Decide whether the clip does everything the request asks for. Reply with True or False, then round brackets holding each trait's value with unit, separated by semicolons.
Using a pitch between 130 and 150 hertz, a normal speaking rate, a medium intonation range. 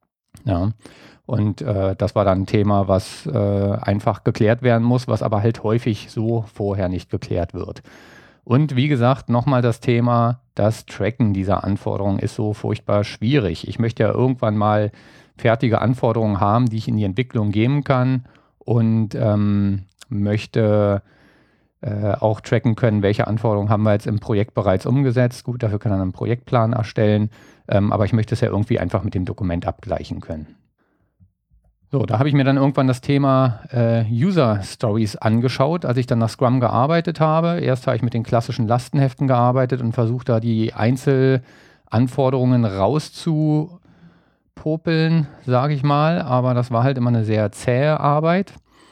False (115 Hz; 160 wpm; 3.6 semitones)